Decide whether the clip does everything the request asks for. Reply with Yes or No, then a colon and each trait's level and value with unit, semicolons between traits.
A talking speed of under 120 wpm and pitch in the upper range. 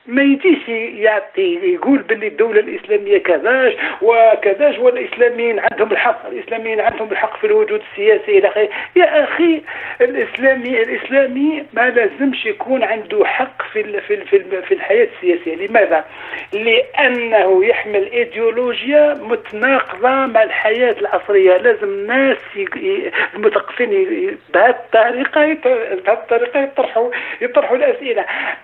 Yes: average, 105 wpm; very high, 300 Hz